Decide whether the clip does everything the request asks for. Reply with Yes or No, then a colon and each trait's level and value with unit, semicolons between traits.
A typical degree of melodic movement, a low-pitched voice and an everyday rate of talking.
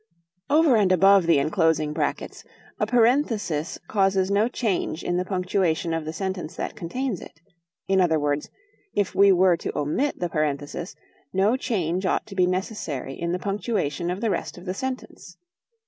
No: average, 3.8 semitones; medium, 185 Hz; average, 170 wpm